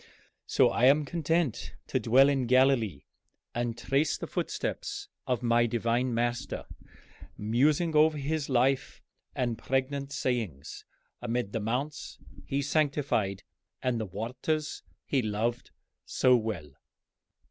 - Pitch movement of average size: Yes, average, 3.3 semitones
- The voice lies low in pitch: Yes, low, 125 Hz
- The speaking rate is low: Yes, slow, 120 wpm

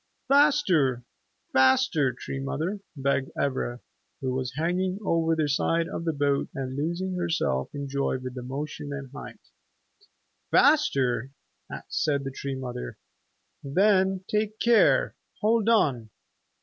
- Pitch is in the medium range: Yes, medium, 145 Hz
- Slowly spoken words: Yes, slow, 125 wpm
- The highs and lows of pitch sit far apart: Yes, wide, 5.8 semitones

